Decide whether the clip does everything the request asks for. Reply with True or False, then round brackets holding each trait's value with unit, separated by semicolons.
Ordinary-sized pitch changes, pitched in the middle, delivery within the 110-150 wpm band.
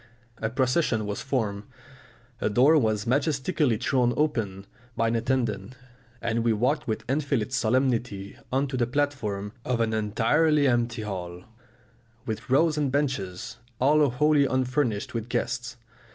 False (4.1 semitones; 125 Hz; 140 wpm)